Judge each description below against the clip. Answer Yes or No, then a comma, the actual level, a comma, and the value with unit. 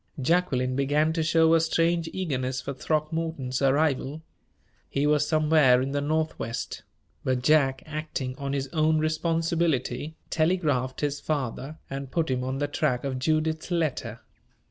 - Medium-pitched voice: Yes, medium, 150 Hz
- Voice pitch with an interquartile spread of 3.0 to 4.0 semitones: Yes, average, 3.3 semitones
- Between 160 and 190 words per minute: No, average, 145 wpm